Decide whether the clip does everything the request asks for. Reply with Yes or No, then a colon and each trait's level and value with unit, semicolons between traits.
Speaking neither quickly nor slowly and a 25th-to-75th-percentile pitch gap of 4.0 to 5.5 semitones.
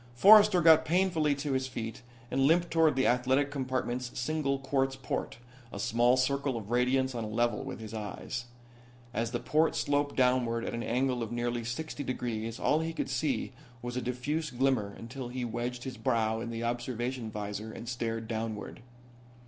No: average, 180 wpm; average, 2.8 semitones